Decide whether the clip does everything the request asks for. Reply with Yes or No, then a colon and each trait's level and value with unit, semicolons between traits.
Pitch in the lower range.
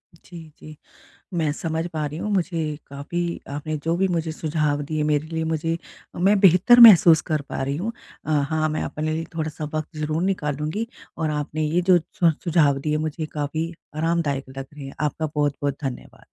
No: medium, 155 Hz